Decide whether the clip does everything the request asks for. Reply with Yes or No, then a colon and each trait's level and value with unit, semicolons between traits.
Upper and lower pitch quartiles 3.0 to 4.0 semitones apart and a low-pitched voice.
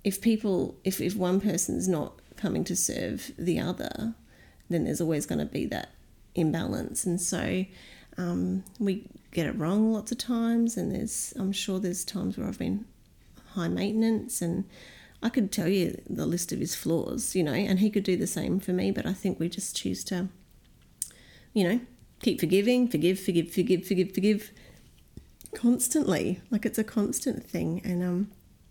No: average, 3.5 semitones; high, 195 Hz